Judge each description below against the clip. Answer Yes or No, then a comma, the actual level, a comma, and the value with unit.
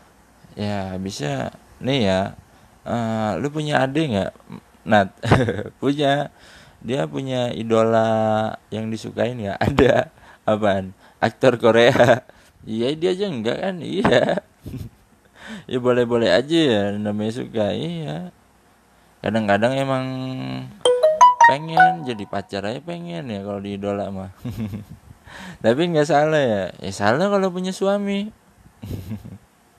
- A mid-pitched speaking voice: No, low, 115 Hz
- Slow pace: No, average, 110 wpm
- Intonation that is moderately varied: No, wide, 6.3 semitones